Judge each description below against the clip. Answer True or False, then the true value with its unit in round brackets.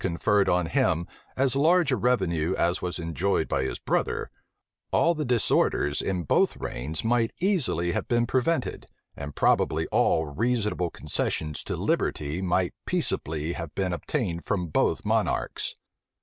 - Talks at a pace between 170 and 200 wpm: False (145 wpm)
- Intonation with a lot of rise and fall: True (6.7 semitones)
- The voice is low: True (90 Hz)